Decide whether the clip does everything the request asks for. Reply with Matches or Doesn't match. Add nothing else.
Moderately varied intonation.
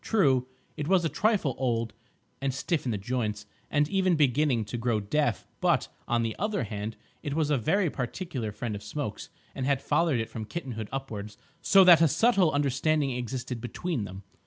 Doesn't match